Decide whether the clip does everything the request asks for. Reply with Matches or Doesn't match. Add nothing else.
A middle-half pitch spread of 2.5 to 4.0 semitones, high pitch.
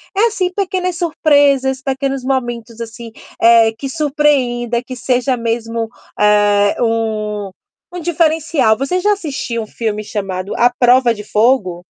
Doesn't match